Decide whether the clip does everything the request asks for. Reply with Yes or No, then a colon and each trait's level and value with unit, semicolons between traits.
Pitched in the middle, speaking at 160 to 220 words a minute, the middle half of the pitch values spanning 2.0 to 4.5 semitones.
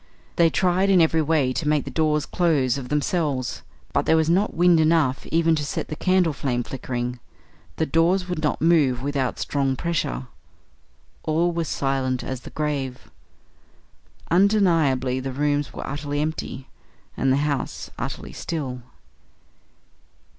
No: medium, 150 Hz; average, 145 wpm; average, 3.8 semitones